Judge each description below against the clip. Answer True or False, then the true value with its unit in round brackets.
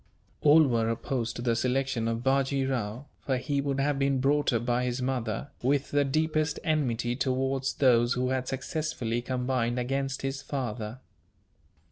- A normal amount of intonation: False (2.3 semitones)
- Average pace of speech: True (160 wpm)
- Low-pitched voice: True (130 Hz)